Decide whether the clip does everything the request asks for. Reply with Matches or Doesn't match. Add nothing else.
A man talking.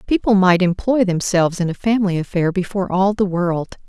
Doesn't match